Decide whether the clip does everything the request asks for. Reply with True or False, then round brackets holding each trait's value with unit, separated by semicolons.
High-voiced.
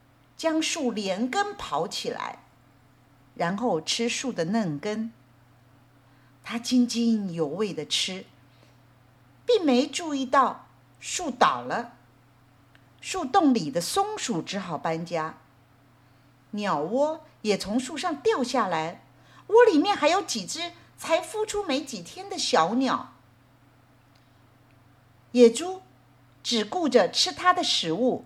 True (215 Hz)